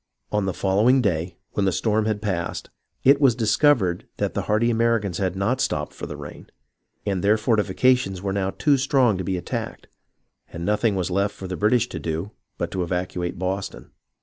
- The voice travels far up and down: No, average, 3.8 semitones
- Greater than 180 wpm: Yes, average, 190 wpm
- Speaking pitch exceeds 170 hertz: No, low, 100 Hz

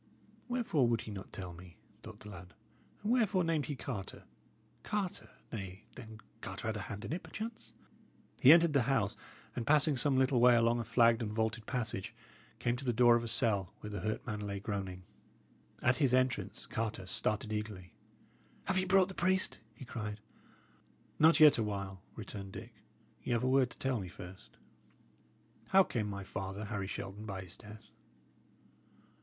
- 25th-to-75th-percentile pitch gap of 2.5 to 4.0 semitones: No, average, 4.6 semitones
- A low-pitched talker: Yes, low, 115 Hz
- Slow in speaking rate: No, average, 180 wpm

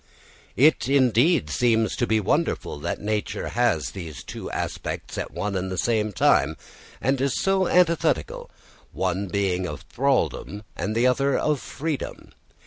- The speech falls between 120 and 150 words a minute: Yes, average, 140 wpm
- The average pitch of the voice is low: Yes, low, 110 Hz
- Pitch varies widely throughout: Yes, wide, 6.5 semitones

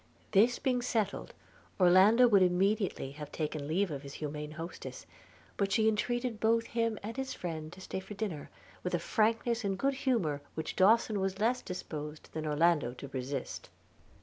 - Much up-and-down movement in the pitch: Yes, wide, 6.5 semitones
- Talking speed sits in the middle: Yes, average, 165 wpm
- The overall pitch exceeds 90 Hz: Yes, high, 190 Hz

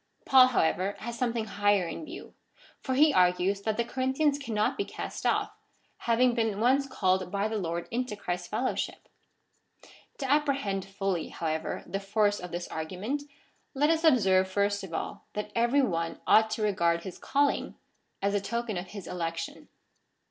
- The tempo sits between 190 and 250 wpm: No, average, 165 wpm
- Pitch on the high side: Yes, high, 210 Hz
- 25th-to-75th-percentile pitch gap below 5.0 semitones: No, average, 5.3 semitones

